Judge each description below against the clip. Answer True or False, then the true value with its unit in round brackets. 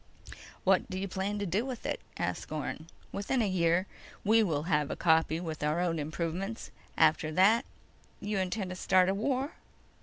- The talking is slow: False (180 wpm)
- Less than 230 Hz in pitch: True (185 Hz)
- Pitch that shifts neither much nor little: True (4.0 semitones)